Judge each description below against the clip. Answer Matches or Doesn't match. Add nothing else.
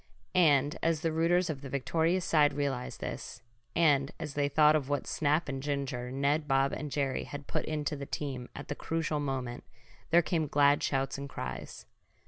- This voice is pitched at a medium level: Matches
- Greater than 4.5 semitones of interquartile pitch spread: Doesn't match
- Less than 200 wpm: Matches